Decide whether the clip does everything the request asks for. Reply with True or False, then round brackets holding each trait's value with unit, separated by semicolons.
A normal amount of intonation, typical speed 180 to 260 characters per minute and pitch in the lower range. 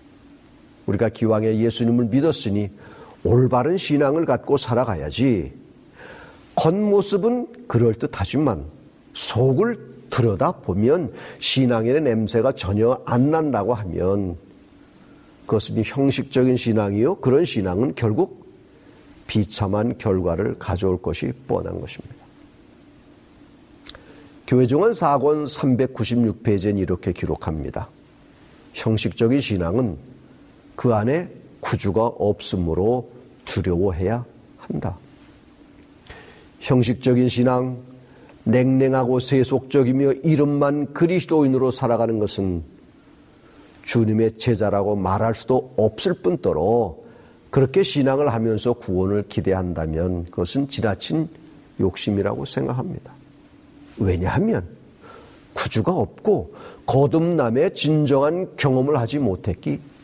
True (5.0 semitones; 240 characters per minute; 120 Hz)